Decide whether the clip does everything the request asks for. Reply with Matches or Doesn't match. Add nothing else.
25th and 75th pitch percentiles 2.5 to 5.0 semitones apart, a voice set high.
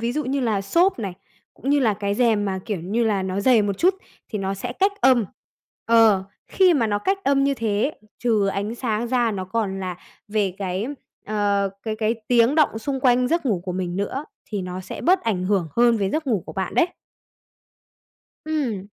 Matches